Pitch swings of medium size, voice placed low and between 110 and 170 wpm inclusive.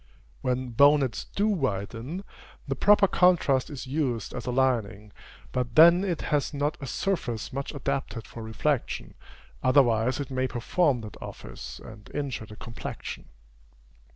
Yes: average, 4.0 semitones; low, 130 Hz; average, 140 wpm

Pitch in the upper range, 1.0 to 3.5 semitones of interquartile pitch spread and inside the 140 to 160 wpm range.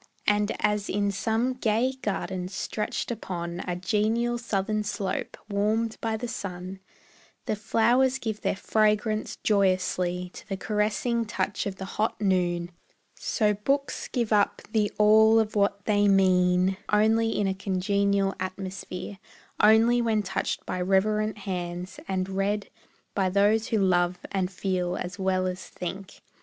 Yes: high, 200 Hz; narrow, 2.5 semitones; average, 145 wpm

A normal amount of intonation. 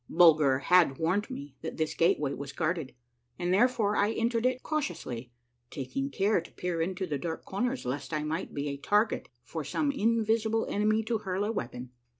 No: wide, 7.3 semitones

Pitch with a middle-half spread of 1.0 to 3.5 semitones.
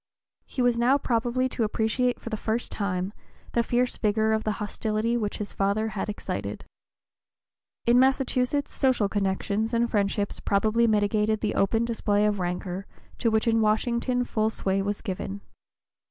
Yes: narrow, 2.5 semitones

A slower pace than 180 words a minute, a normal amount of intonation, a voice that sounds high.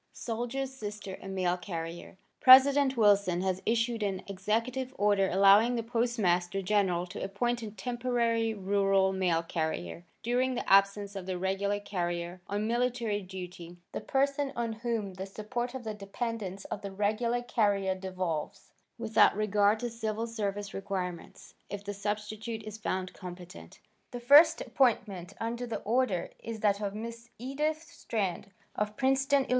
Yes: average, 150 wpm; average, 3.8 semitones; high, 210 Hz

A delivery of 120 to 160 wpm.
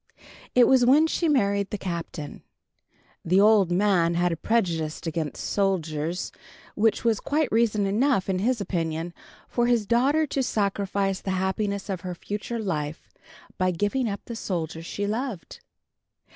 Yes: average, 150 wpm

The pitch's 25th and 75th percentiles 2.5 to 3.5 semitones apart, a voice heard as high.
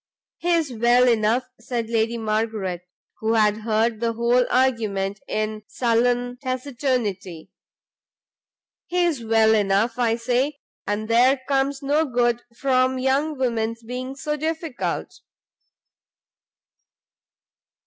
Yes: average, 2.9 semitones; high, 240 Hz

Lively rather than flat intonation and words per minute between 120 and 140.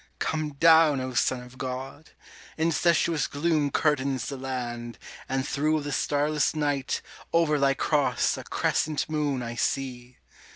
No: average, 2.9 semitones; slow, 135 wpm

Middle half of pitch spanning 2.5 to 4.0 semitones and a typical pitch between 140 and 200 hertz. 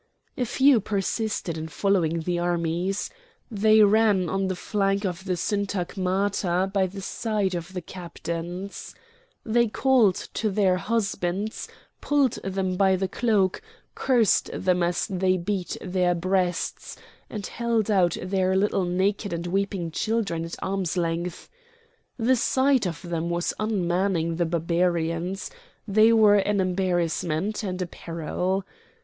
Yes: average, 2.9 semitones; high, 190 Hz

